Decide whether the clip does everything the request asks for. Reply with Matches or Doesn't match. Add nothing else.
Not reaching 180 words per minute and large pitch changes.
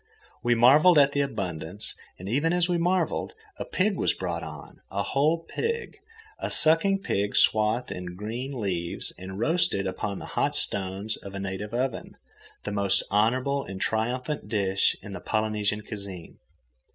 Matches